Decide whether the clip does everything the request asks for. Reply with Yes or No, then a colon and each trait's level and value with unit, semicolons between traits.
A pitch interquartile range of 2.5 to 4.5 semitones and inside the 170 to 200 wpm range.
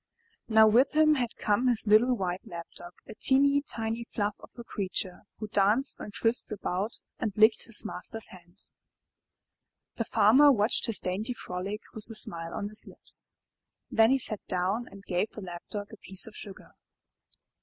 Yes: average, 3.3 semitones; average, 175 wpm